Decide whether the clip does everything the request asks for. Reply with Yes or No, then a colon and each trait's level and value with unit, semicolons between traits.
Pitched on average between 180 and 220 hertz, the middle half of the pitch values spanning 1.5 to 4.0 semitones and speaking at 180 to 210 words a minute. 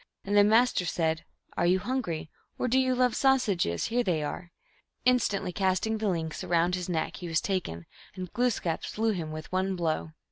No: medium, 185 Hz; average, 5.1 semitones; average, 200 wpm